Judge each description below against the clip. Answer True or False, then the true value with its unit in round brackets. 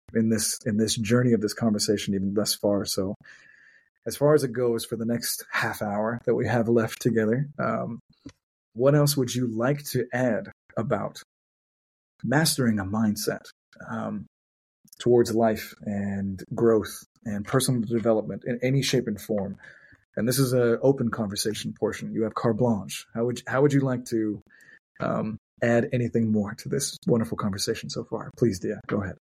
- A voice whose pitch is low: True (115 Hz)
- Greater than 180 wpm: False (175 wpm)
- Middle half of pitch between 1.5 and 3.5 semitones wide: True (2.7 semitones)